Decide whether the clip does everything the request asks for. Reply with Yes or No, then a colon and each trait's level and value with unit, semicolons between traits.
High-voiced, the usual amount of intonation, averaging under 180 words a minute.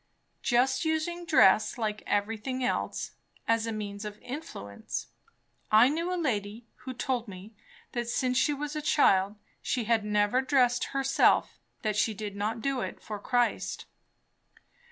Yes: high, 235 Hz; average, 4.2 semitones; average, 150 wpm